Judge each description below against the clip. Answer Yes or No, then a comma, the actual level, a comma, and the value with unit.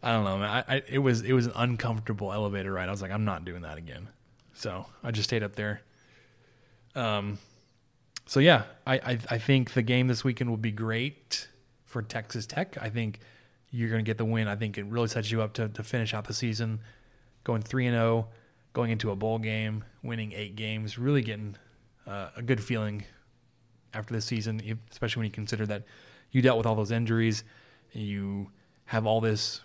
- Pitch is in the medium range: No, low, 115 Hz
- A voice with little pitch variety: Yes, narrow, 2.1 semitones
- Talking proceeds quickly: Yes, fast, 210 wpm